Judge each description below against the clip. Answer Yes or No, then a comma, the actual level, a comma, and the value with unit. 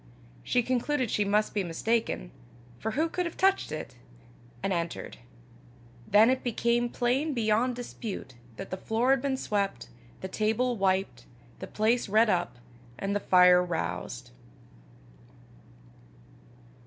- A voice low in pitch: No, high, 215 Hz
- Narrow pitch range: No, average, 4.8 semitones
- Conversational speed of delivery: No, slow, 130 wpm